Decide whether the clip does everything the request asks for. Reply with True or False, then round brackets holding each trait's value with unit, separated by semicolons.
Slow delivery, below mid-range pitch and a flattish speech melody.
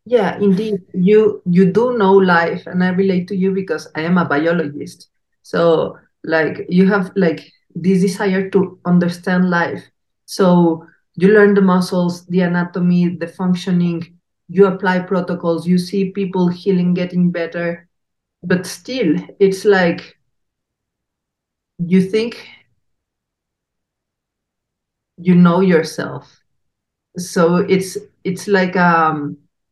False (120 wpm; 180 Hz; 2.0 semitones)